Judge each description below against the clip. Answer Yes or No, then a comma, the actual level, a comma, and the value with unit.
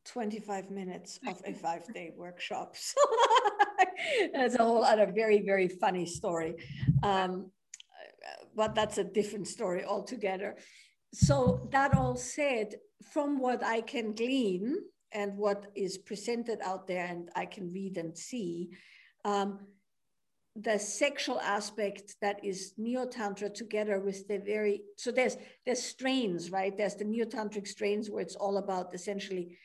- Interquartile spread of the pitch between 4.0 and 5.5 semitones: No, average, 3.4 semitones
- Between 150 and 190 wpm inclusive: No, average, 140 wpm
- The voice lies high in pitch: Yes, high, 205 Hz